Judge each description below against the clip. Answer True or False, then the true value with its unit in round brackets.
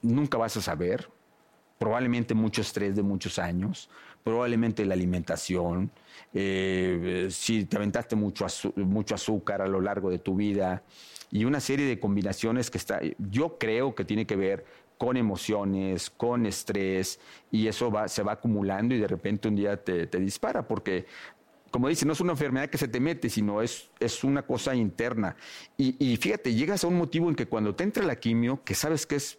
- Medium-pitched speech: False (110 Hz)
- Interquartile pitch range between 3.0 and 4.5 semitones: True (4.0 semitones)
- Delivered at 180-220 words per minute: True (185 wpm)